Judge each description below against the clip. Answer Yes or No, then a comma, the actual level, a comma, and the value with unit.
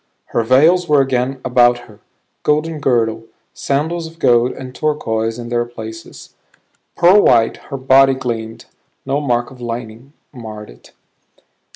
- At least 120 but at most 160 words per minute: Yes, average, 140 wpm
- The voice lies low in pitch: Yes, low, 125 Hz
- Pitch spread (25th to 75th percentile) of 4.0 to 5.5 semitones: No, average, 3.5 semitones